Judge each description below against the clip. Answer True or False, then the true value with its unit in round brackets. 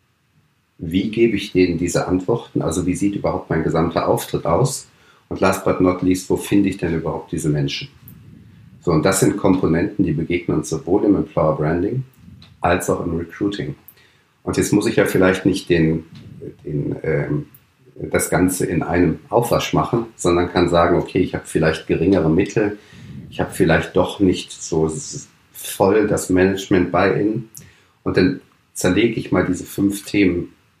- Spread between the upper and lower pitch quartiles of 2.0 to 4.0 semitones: True (2.9 semitones)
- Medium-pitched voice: False (90 Hz)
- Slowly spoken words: False (170 wpm)